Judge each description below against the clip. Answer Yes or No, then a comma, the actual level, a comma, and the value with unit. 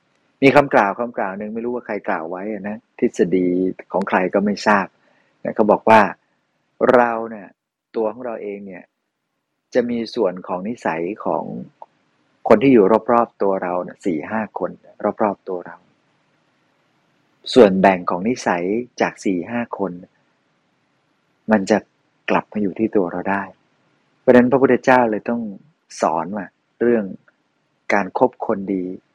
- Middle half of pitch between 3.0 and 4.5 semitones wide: Yes, average, 3.6 semitones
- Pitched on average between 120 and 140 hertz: No, low, 105 Hz